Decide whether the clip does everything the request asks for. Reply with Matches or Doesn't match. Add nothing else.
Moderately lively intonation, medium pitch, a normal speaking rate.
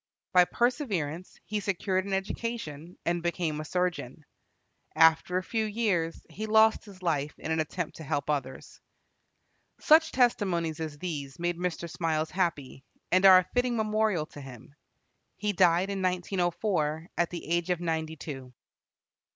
Matches